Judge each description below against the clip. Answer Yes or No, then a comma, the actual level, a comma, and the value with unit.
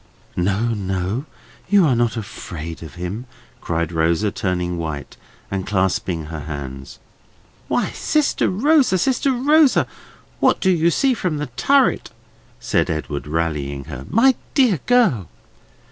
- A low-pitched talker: Yes, low, 100 Hz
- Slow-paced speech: Yes, slow, 130 wpm